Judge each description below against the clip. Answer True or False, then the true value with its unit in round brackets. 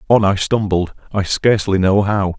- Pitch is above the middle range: False (100 Hz)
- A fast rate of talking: False (175 wpm)